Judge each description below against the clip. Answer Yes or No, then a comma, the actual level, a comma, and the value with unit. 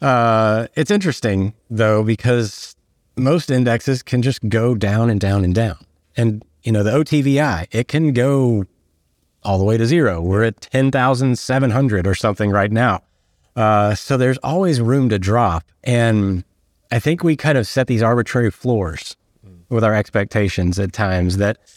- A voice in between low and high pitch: No, low, 115 Hz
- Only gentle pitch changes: No, average, 4.4 semitones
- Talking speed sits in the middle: Yes, average, 160 wpm